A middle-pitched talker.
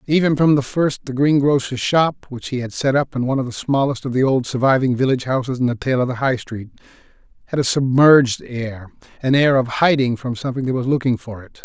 No: low, 130 Hz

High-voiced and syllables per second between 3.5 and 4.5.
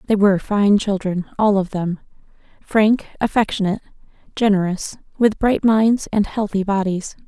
No: high, 205 Hz; 4.9 syllables/s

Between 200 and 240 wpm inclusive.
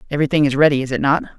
No: fast, 260 wpm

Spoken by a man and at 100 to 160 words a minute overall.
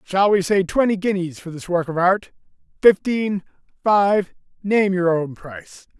Yes: male; average, 150 wpm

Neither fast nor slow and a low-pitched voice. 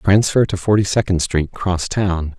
Yes: average, 150 wpm; very low, 95 Hz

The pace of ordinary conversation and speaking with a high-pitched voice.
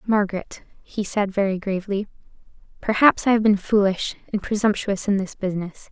Yes: average, 150 wpm; high, 200 Hz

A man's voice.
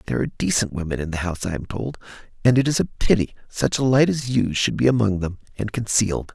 Yes: male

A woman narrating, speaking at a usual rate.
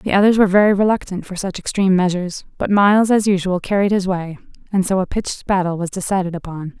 No: female; fast, 210 wpm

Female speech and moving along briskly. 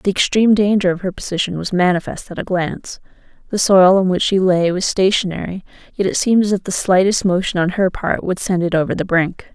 Yes: female; fast, 225 wpm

